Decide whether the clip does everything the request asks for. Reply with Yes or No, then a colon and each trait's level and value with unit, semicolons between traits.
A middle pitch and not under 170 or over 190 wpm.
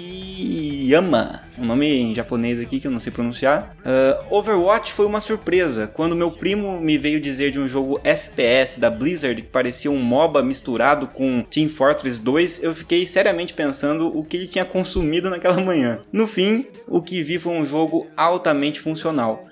Yes: medium, 155 Hz; average, 180 wpm